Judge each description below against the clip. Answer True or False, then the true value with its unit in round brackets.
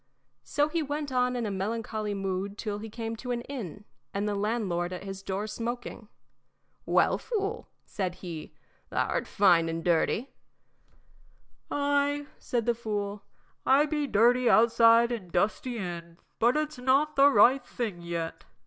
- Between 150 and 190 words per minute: True (155 wpm)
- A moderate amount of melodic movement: True (4.6 semitones)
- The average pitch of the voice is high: True (225 Hz)